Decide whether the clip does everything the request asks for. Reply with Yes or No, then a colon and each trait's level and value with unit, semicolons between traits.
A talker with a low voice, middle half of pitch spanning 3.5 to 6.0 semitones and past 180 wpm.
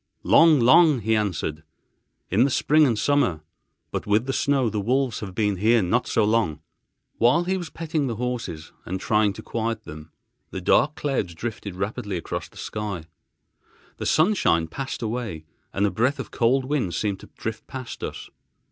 No: low, 115 Hz; average, 5.3 semitones; average, 175 wpm